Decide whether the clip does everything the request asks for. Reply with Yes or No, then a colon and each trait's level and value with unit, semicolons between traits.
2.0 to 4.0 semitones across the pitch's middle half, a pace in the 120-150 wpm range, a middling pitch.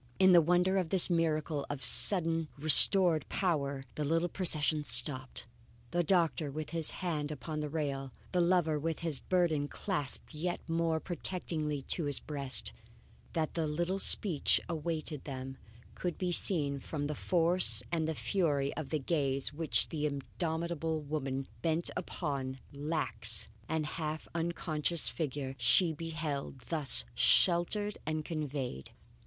Yes: average, 2.9 semitones; average, 140 wpm; medium, 155 Hz